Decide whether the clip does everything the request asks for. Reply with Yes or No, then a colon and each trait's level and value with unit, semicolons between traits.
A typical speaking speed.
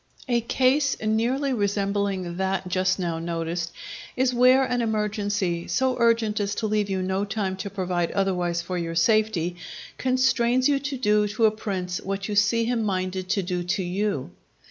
Yes: average, 170 wpm